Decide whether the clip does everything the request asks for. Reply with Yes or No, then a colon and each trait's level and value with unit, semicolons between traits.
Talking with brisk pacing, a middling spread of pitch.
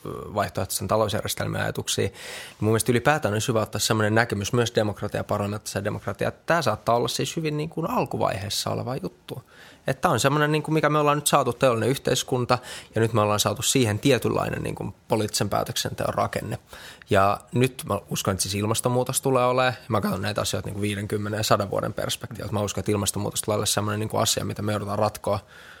Yes: fast, 185 wpm; average, 3.6 semitones